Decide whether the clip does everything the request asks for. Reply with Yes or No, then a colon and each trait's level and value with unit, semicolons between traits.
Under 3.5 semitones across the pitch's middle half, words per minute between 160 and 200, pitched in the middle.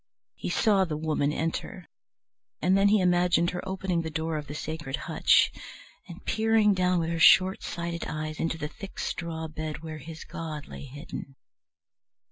Yes: average, 2.8 semitones; average, 170 wpm; medium, 165 Hz